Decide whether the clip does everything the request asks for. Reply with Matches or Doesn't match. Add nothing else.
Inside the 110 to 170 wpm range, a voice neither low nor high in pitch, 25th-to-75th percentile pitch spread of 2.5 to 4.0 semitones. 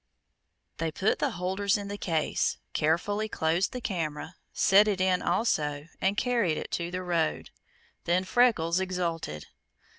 Matches